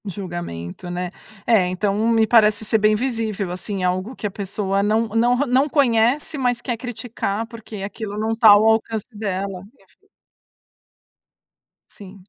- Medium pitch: No, high, 215 Hz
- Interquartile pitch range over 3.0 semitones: No, average, 2.7 semitones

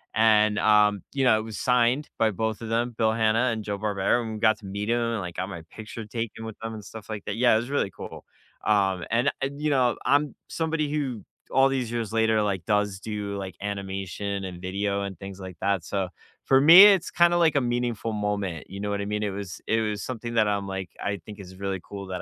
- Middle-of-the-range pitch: No, low, 105 Hz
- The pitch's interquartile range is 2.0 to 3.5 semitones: Yes, average, 3.0 semitones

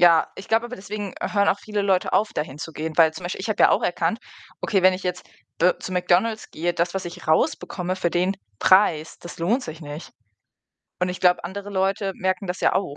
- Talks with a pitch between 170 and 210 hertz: Yes, medium, 185 Hz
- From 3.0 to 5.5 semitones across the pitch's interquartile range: No, narrow, 2.4 semitones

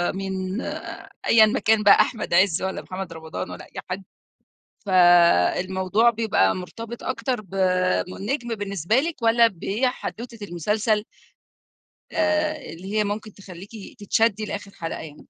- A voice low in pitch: No, high, 205 Hz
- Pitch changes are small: No, average, 3.6 semitones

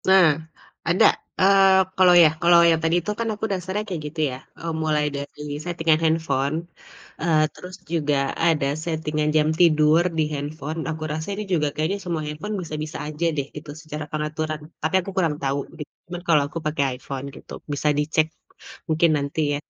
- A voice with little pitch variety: Yes, narrow, 2.3 semitones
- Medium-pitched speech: Yes, medium, 155 Hz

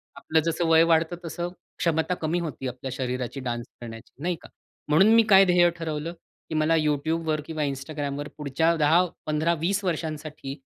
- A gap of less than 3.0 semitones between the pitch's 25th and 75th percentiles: Yes, narrow, 2.5 semitones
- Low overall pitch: No, medium, 155 Hz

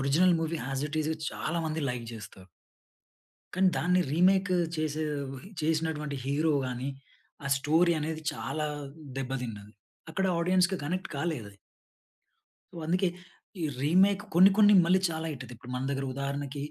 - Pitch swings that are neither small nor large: Yes, average, 4.4 semitones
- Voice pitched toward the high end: No, medium, 155 Hz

